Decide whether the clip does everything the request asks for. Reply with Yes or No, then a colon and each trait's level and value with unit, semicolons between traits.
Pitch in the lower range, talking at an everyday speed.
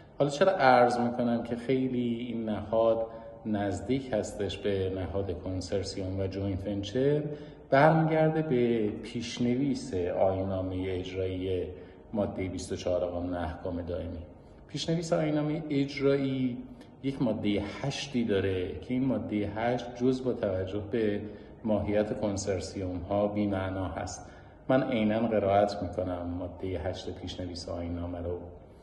Yes: low, 105 Hz; average, 115 wpm